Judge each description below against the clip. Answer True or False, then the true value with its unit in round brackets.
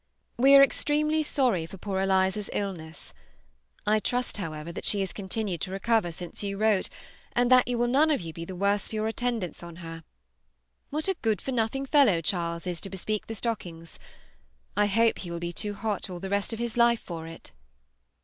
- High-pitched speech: True (205 Hz)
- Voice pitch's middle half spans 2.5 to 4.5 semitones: False (5.1 semitones)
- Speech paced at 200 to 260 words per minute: True (205 wpm)